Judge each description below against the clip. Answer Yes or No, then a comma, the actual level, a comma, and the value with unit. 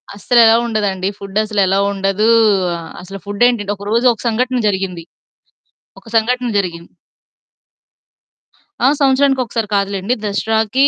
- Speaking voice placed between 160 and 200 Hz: No, high, 210 Hz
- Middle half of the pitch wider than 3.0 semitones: Yes, average, 3.4 semitones